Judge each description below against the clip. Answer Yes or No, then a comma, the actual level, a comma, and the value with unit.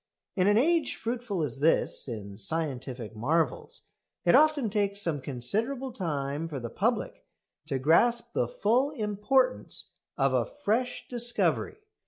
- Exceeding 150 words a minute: No, slow, 135 wpm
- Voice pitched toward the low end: No, high, 200 Hz